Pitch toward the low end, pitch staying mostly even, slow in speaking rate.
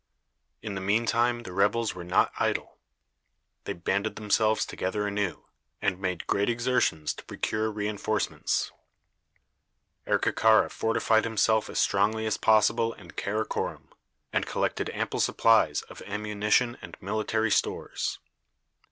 Yes: low, 105 Hz; narrow, 1.8 semitones; slow, 125 wpm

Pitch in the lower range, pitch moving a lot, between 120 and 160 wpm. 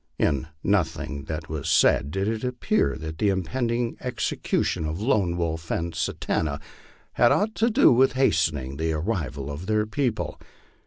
Yes: very low, 85 Hz; wide, 7.0 semitones; average, 155 wpm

